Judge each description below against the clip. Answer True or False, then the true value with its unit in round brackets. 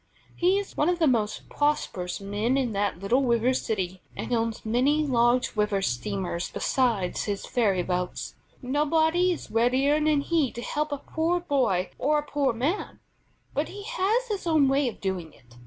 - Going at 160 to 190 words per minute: True (175 wpm)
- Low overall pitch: False (255 Hz)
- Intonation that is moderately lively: False (6.7 semitones)